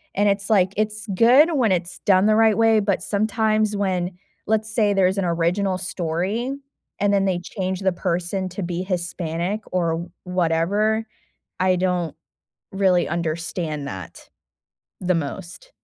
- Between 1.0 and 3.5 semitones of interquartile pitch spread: Yes, average, 3.2 semitones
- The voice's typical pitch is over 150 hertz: Yes, medium, 185 Hz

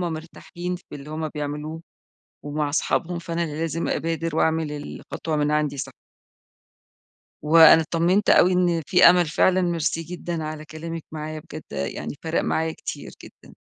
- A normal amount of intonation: No, narrow, 1.9 semitones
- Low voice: No, medium, 160 Hz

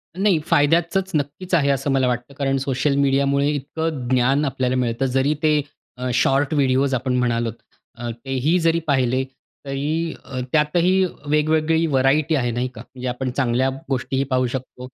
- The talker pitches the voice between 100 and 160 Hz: Yes, low, 135 Hz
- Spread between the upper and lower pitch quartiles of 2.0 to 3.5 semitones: Yes, average, 2.9 semitones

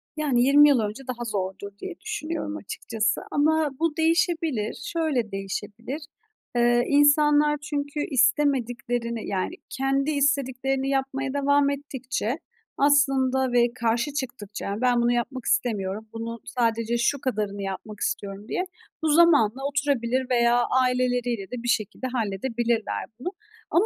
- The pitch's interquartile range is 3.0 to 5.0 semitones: Yes, average, 3.7 semitones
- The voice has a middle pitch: No, very high, 255 Hz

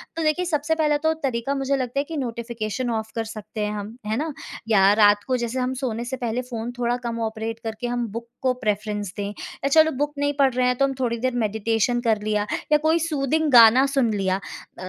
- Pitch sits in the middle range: No, high, 240 Hz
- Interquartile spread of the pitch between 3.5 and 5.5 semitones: Yes, average, 3.9 semitones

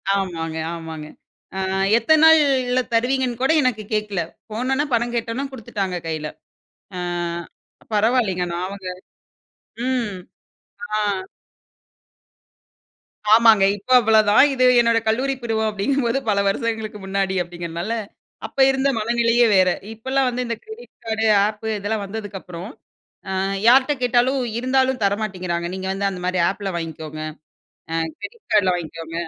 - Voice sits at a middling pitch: No, high, 220 Hz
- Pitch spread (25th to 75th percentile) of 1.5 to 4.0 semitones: No, average, 4.7 semitones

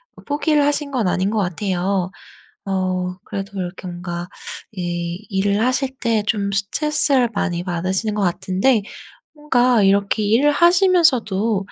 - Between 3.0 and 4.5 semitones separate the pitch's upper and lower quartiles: No, wide, 5.5 semitones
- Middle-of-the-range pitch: No, high, 200 Hz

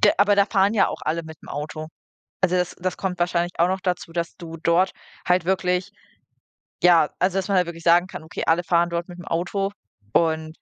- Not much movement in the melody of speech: Yes, narrow, 1.9 semitones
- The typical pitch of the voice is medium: Yes, medium, 175 Hz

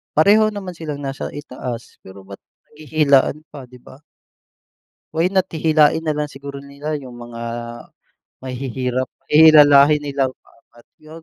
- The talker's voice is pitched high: No, medium, 145 Hz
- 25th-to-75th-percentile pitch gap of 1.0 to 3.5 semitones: Yes, average, 3.1 semitones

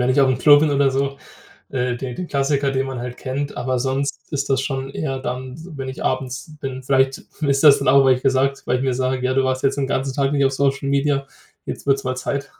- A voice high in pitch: No, low, 135 Hz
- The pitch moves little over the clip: Yes, narrow, 1.1 semitones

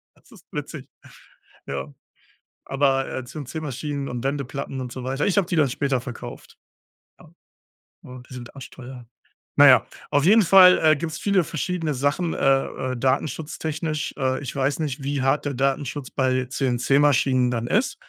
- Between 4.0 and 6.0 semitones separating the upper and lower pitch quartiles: No, average, 2.9 semitones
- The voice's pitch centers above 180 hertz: No, low, 135 Hz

